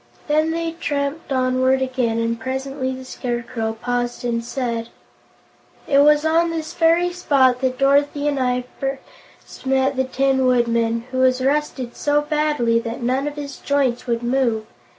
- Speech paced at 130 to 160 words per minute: Yes, average, 155 wpm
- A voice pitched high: Yes, very high, 260 Hz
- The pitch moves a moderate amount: Yes, average, 3.0 semitones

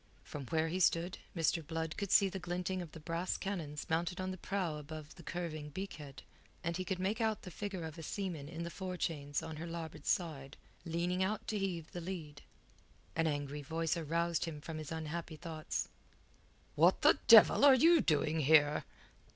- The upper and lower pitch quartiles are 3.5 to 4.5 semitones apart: No, average, 2.8 semitones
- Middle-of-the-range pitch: Yes, medium, 165 Hz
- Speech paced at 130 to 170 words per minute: No, average, 190 wpm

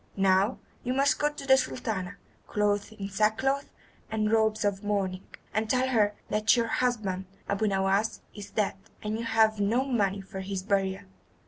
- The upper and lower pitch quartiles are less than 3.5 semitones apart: Yes, average, 2.7 semitones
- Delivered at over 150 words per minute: Yes, average, 165 wpm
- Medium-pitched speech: No, high, 210 Hz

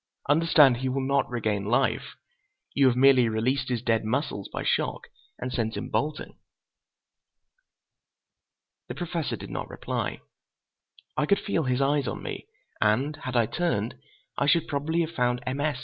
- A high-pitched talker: No, low, 130 Hz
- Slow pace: No, average, 160 wpm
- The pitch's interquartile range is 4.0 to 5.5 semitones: No, average, 3.5 semitones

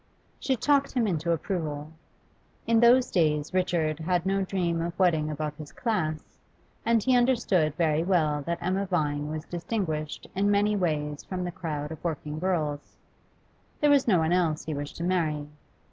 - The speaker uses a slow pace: No, average, 170 wpm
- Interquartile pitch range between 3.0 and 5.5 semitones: Yes, average, 4.1 semitones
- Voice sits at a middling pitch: Yes, medium, 170 Hz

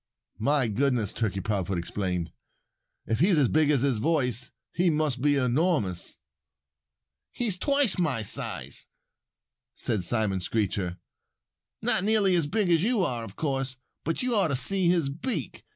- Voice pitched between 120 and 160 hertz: Yes, medium, 140 Hz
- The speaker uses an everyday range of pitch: No, wide, 8.0 semitones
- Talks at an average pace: Yes, average, 150 wpm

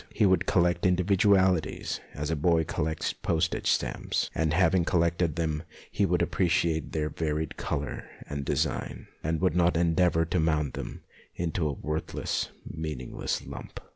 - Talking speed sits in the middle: Yes, average, 155 wpm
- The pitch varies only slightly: Yes, narrow, 2.2 semitones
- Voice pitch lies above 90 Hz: No, very low, 80 Hz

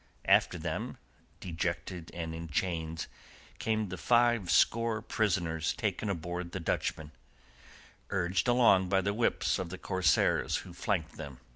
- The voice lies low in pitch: Yes, very low, 90 Hz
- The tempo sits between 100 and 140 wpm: Yes, slow, 135 wpm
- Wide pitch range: No, average, 3.7 semitones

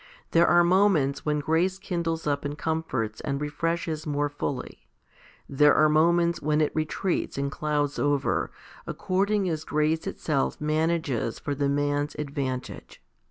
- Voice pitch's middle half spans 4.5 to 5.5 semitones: No, narrow, 2.5 semitones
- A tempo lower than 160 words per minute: Yes, average, 140 wpm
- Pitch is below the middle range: No, medium, 150 Hz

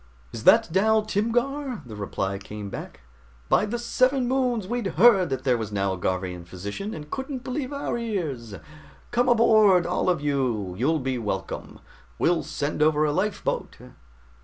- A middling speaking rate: Yes, average, 160 wpm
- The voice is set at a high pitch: No, medium, 175 Hz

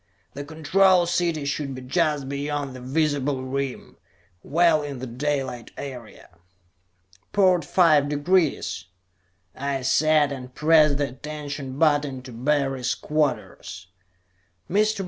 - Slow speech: Yes, slow, 115 wpm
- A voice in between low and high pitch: Yes, medium, 145 Hz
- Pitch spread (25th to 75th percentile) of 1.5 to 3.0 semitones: Yes, average, 2.7 semitones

